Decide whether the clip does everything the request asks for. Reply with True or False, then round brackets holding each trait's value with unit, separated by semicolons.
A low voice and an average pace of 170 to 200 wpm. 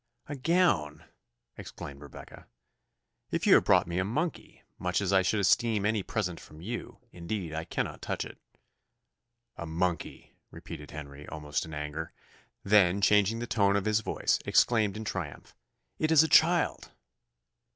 False (100 Hz; 155 wpm)